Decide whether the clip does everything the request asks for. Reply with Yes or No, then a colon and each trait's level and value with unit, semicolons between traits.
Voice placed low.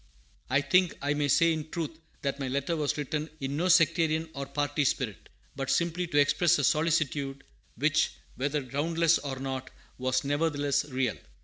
No: medium, 145 Hz